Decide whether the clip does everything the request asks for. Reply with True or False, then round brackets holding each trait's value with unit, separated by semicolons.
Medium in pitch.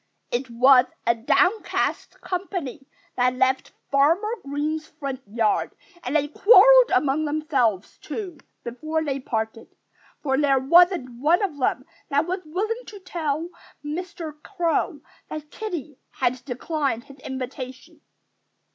False (290 Hz)